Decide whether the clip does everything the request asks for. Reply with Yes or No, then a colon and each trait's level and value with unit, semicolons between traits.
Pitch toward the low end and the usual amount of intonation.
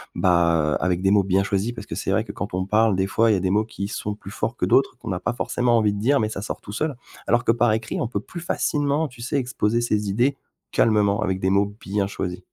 Yes: low, 105 Hz; average, 3.5 semitones